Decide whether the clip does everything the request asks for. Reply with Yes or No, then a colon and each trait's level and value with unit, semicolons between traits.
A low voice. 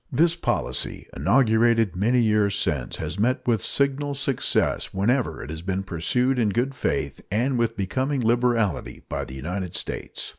Yes: low, 115 Hz